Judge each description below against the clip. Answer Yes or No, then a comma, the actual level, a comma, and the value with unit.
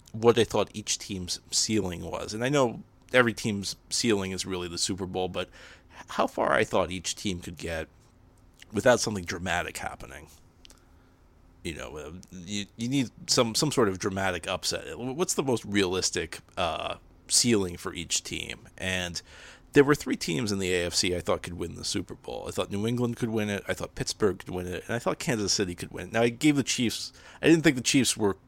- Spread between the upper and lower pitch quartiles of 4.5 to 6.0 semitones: Yes, average, 4.9 semitones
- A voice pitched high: No, very low, 95 Hz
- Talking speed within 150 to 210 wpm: Yes, fast, 205 wpm